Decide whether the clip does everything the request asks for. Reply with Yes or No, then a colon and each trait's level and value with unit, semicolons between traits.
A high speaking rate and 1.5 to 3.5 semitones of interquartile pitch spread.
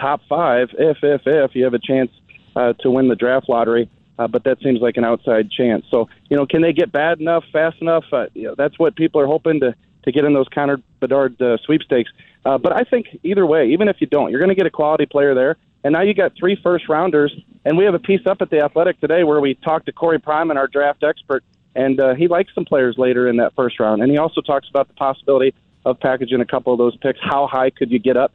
No: fast, 265 wpm; average, 3.9 semitones